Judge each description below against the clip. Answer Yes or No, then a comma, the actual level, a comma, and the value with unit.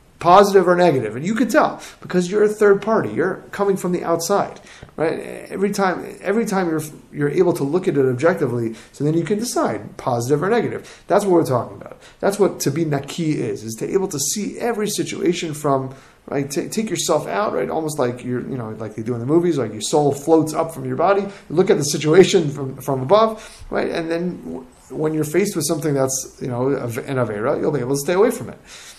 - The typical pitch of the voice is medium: Yes, medium, 165 Hz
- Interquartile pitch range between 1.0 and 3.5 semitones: No, wide, 5.5 semitones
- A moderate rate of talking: No, fast, 230 wpm